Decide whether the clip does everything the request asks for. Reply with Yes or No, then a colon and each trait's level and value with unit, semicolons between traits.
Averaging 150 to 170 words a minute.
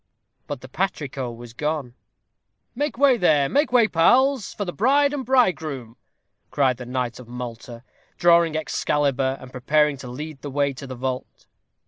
Yes: average, 160 wpm